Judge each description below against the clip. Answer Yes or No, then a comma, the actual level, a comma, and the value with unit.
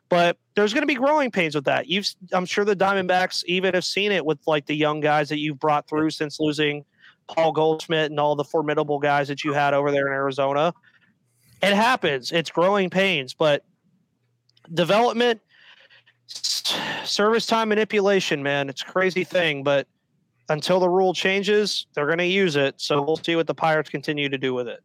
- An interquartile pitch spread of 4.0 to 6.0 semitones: Yes, average, 4.5 semitones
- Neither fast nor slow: Yes, average, 190 wpm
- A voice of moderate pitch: Yes, medium, 160 Hz